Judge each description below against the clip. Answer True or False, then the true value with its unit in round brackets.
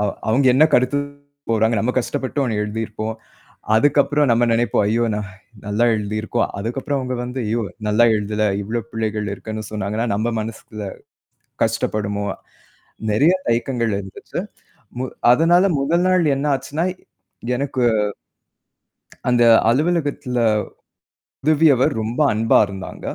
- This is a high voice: False (120 Hz)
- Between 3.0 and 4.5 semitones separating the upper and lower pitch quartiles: True (4.2 semitones)